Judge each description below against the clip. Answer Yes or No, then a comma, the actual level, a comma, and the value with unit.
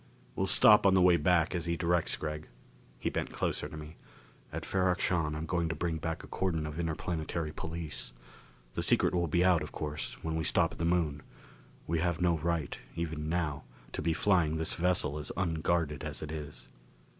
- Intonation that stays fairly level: Yes, narrow, 2.1 semitones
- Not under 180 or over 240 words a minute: Yes, average, 200 wpm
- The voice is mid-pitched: No, very low, 80 Hz